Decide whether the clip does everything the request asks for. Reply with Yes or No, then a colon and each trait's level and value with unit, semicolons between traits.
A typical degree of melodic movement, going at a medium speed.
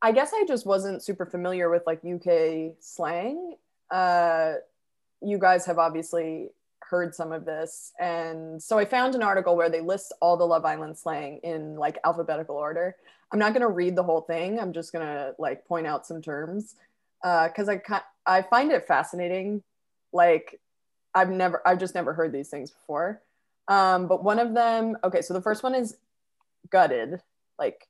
Yes: average, 4.0 semitones; average, 180 wpm